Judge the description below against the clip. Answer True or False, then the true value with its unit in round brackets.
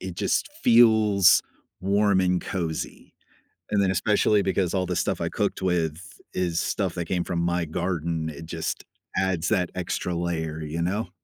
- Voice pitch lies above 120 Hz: False (90 Hz)